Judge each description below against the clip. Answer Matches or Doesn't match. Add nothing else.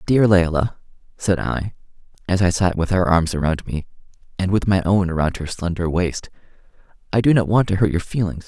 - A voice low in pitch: Matches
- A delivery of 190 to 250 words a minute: Matches